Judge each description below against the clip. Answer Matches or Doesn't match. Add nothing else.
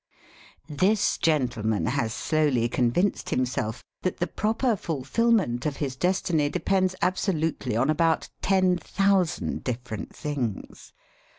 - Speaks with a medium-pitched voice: Matches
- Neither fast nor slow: Doesn't match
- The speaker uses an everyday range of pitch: Doesn't match